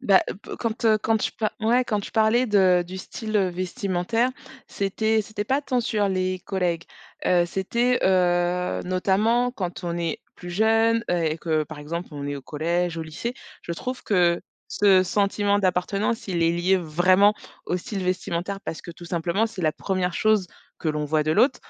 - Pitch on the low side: No, medium, 185 Hz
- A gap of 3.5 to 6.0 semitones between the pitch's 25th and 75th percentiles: Yes, average, 3.9 semitones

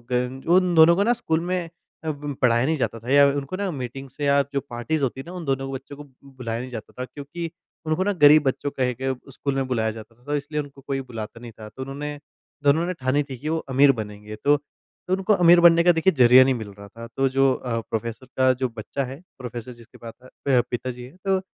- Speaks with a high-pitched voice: No, low, 135 Hz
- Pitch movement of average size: Yes, average, 3.5 semitones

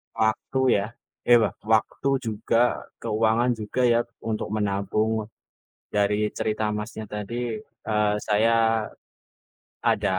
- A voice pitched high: No, low, 110 Hz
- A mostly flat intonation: Yes, narrow, 1.4 semitones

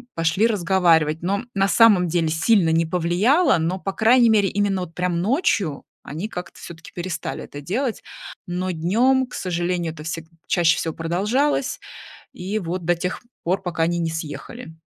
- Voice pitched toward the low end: No, medium, 180 Hz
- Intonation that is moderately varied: Yes, average, 3.9 semitones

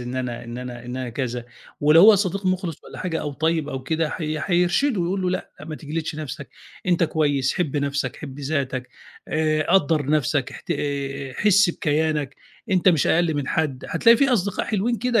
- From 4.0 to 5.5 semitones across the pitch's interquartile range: Yes, average, 4.5 semitones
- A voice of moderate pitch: Yes, medium, 155 Hz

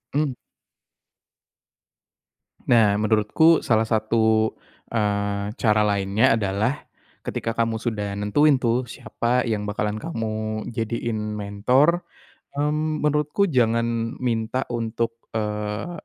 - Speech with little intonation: No, average, 3.0 semitones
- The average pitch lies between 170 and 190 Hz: No, low, 115 Hz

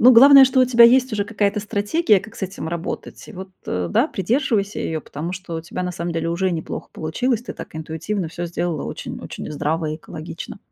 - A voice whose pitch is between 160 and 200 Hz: Yes, high, 190 Hz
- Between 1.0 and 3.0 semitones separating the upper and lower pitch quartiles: No, wide, 5.6 semitones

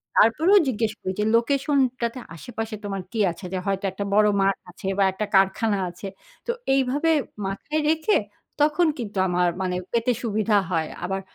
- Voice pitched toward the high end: Yes, high, 215 Hz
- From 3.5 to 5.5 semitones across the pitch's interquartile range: Yes, average, 5.1 semitones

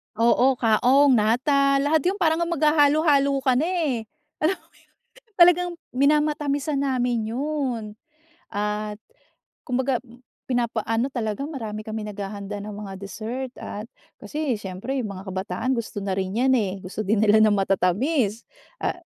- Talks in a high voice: Yes, high, 245 Hz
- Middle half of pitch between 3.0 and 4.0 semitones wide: No, average, 5.2 semitones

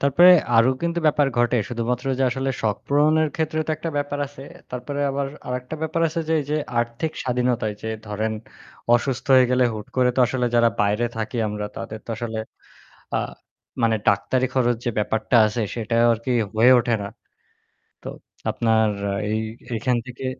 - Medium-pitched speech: No, low, 125 Hz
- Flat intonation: No, average, 3.6 semitones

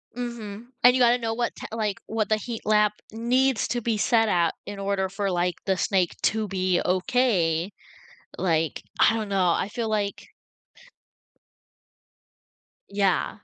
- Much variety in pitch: No, average, 3.3 semitones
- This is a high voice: Yes, high, 210 Hz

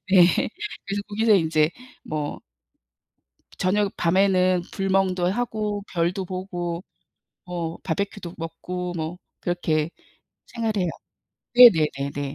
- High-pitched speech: No, medium, 180 Hz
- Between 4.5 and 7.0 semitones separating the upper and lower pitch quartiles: No, average, 2.9 semitones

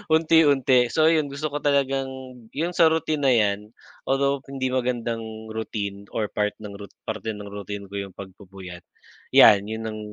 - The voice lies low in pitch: Yes, low, 115 Hz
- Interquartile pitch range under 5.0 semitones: No, average, 5.3 semitones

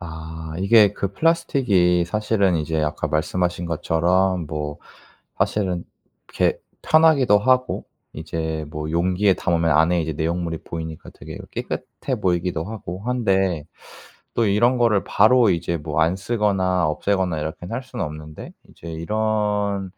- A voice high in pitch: No, very low, 90 Hz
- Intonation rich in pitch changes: No, average, 4.5 semitones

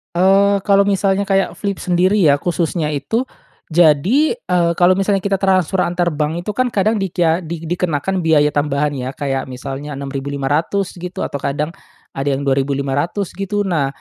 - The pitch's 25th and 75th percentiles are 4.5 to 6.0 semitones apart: Yes, average, 5.2 semitones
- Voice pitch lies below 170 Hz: No, medium, 175 Hz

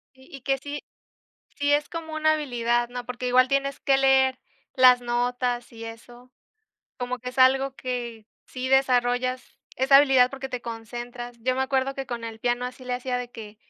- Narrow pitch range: Yes, narrow, 1.7 semitones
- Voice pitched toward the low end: No, very high, 250 Hz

